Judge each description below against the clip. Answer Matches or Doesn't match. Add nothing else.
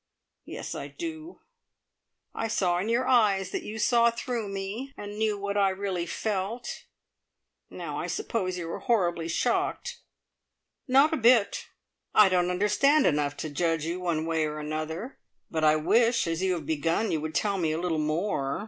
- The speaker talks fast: Doesn't match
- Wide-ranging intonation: Matches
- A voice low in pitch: Doesn't match